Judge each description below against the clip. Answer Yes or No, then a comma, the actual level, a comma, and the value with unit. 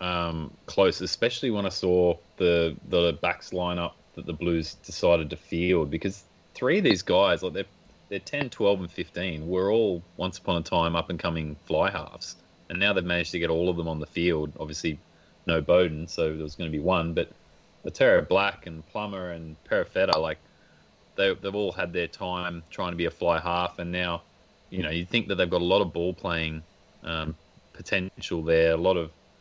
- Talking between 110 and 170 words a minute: No, fast, 205 wpm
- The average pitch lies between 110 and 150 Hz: No, very low, 85 Hz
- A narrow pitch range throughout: Yes, narrow, 1.8 semitones